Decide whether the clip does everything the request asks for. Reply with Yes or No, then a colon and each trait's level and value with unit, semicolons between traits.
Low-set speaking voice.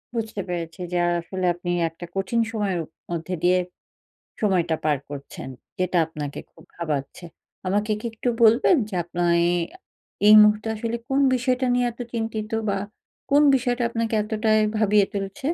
No: high, 205 Hz